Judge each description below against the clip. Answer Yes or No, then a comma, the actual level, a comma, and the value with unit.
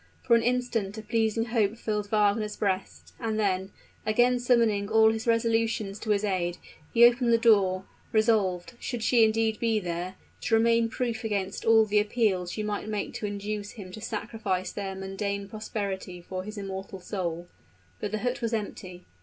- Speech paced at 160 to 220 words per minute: Yes, average, 175 wpm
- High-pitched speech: Yes, high, 215 Hz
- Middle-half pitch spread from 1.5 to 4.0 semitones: Yes, narrow, 2.5 semitones